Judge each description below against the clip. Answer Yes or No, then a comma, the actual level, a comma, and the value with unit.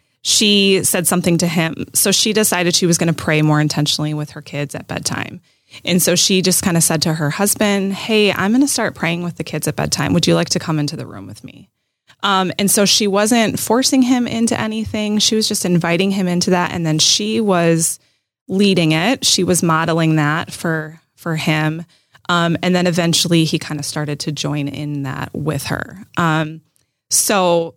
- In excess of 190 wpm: Yes, fast, 205 wpm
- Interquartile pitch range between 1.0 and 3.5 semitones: No, average, 4.0 semitones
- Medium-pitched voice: Yes, medium, 170 Hz